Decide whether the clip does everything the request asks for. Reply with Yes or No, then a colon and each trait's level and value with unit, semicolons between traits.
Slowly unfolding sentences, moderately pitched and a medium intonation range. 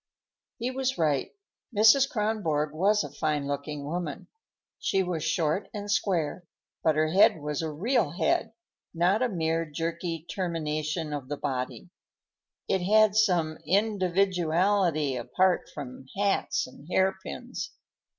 Yes: slow, 130 wpm; medium, 170 Hz; average, 4.7 semitones